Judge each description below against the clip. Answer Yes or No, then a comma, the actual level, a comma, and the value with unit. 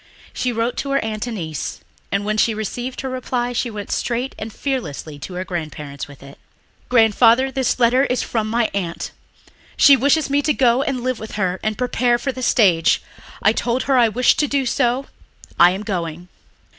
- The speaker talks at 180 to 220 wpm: Yes, average, 195 wpm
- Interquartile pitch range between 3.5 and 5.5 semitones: Yes, average, 4.4 semitones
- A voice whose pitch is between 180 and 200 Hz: No, high, 235 Hz